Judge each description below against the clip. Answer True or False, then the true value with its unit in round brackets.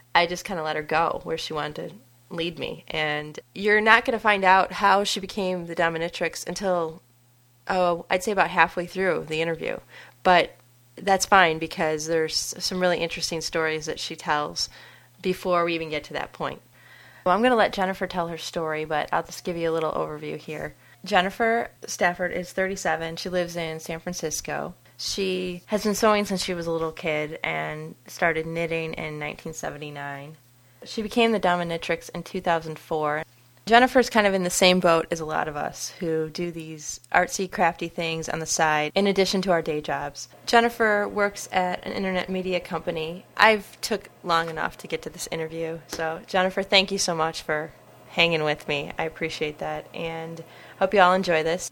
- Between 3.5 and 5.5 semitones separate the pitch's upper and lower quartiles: False (3.0 semitones)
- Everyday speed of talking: True (190 wpm)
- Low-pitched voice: False (170 Hz)